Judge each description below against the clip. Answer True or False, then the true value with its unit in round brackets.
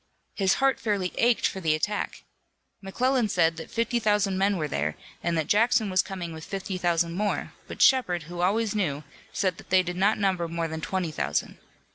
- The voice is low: False (185 Hz)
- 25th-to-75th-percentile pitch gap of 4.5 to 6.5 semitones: False (3.7 semitones)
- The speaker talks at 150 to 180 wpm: False (195 wpm)